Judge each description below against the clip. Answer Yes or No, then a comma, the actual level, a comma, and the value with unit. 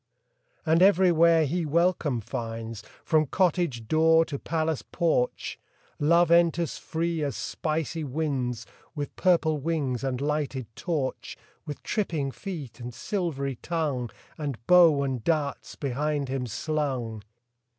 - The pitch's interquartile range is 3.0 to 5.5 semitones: Yes, average, 4.0 semitones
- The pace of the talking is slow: Yes, slow, 120 wpm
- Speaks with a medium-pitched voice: Yes, medium, 150 Hz